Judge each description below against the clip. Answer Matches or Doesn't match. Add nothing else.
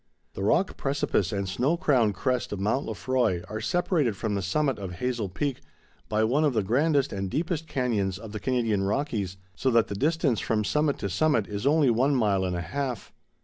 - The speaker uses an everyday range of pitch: Doesn't match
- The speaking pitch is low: Matches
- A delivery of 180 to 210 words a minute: Matches